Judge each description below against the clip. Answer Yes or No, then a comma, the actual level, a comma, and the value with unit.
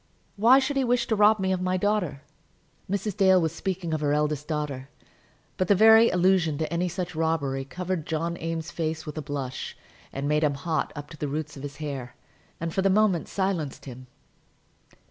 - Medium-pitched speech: Yes, medium, 165 Hz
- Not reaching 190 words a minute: No, average, 195 wpm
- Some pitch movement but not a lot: Yes, average, 4.2 semitones